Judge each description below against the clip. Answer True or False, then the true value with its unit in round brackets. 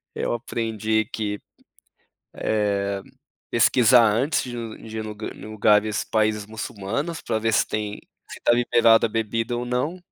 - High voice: False (110 Hz)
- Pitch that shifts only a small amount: True (1.9 semitones)